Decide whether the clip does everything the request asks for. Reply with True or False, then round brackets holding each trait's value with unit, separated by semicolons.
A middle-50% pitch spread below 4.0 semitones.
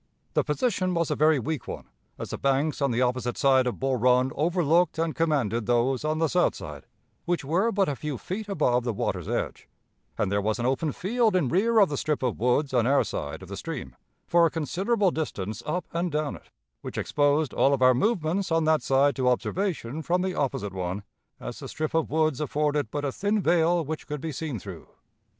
False (4.9 semitones)